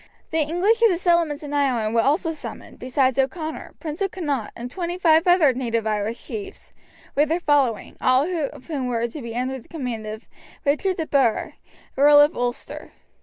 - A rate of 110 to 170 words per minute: No, average, 185 wpm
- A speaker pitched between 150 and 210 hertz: No, very high, 290 Hz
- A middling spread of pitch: Yes, average, 5.0 semitones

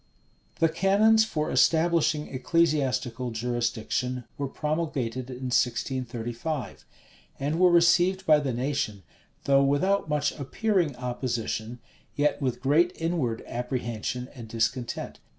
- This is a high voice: No, low, 135 Hz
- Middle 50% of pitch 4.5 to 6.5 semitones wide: Yes, average, 4.9 semitones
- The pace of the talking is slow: Yes, slow, 110 wpm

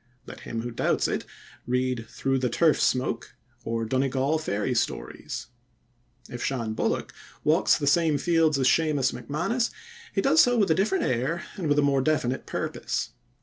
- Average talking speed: Yes, average, 165 wpm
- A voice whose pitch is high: No, low, 135 Hz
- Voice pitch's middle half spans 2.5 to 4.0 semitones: No, average, 4.4 semitones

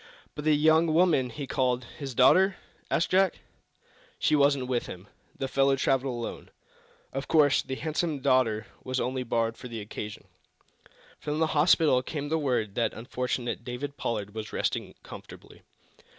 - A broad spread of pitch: No, average, 3.6 semitones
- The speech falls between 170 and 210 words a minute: No, average, 155 wpm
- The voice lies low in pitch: Yes, low, 130 Hz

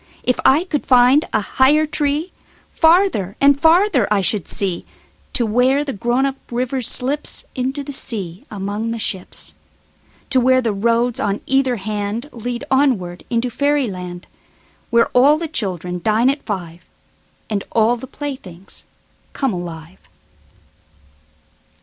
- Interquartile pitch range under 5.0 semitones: No, wide, 5.4 semitones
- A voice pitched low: No, high, 245 Hz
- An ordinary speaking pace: No, slow, 120 wpm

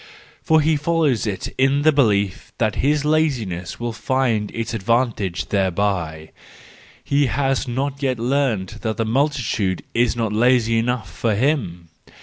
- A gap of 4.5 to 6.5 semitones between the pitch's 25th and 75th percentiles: Yes, average, 5.0 semitones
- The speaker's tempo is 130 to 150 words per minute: Yes, average, 140 wpm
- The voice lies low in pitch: Yes, low, 120 Hz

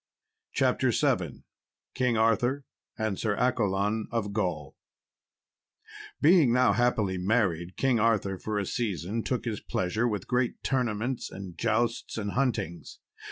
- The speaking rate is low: Yes, slow, 125 wpm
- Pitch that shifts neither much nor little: Yes, average, 3.8 semitones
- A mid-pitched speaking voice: No, low, 110 Hz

